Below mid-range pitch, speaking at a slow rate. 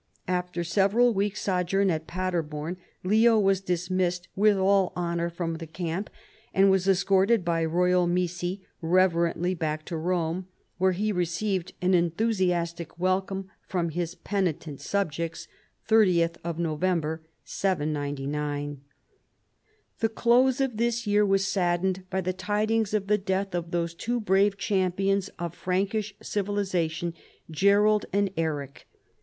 No: medium, 185 Hz; slow, 125 wpm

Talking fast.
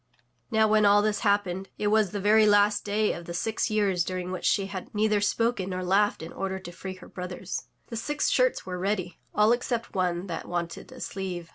Yes: fast, 225 wpm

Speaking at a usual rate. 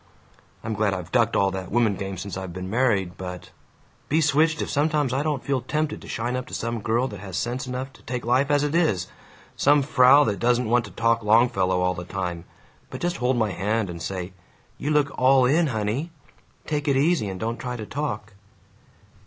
No: fast, 210 wpm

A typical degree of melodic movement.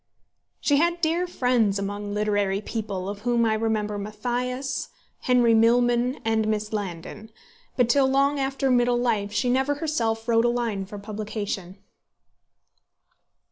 Yes: average, 3.3 semitones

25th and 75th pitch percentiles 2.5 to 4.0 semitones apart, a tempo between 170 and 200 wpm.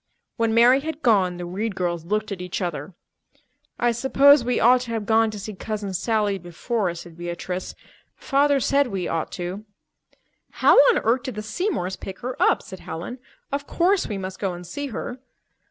No: wide, 5.6 semitones; average, 185 wpm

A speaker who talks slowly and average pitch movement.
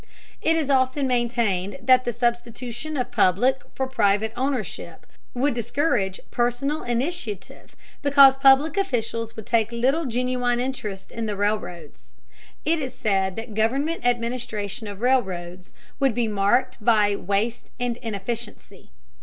Yes: slow, 130 wpm; average, 3.8 semitones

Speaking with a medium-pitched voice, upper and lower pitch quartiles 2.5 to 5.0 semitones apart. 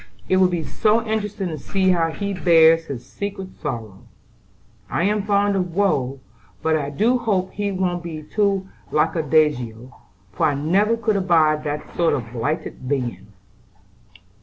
No: medium, 170 Hz; wide, 5.4 semitones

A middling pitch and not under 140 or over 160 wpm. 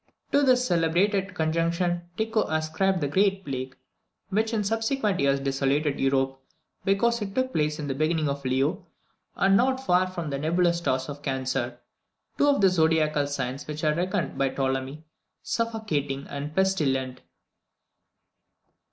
Yes: medium, 160 Hz; average, 145 wpm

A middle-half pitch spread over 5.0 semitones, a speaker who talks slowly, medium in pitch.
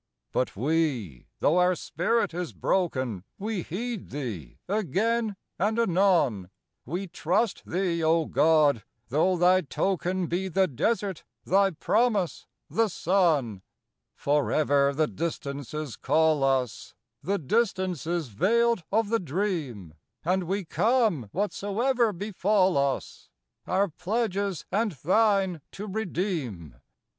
Yes: wide, 5.4 semitones; slow, 115 wpm; medium, 180 Hz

